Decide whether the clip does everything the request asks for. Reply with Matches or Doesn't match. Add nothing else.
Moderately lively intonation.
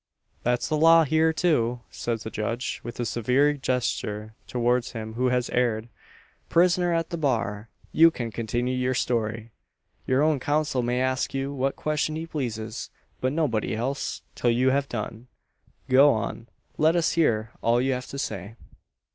Matches